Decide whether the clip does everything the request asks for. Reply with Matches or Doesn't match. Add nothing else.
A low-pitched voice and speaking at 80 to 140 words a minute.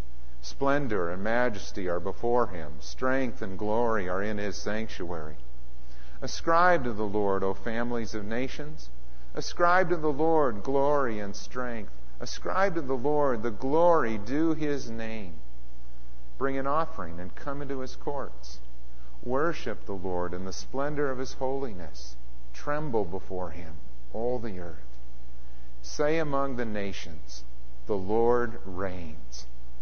Matches